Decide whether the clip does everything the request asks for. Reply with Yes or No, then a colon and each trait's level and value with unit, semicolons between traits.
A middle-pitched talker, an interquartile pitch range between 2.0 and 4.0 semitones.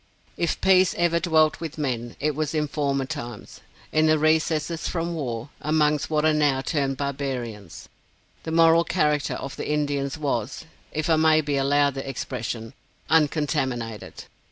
Yes: medium, 150 Hz; narrow, 2.6 semitones